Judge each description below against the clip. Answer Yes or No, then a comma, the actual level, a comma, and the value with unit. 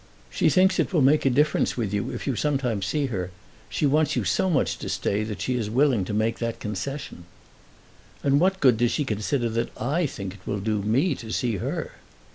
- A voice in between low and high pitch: No, low, 120 Hz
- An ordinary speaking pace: No, fast, 220 wpm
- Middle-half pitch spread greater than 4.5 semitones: Yes, average, 5.3 semitones